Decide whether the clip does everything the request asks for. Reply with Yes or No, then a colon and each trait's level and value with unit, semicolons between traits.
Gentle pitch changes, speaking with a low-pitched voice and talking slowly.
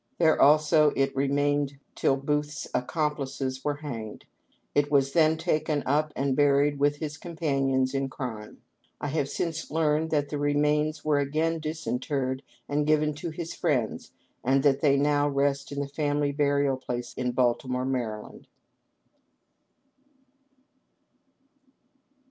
No: narrow, 2.0 semitones; medium, 145 Hz; slow, 130 wpm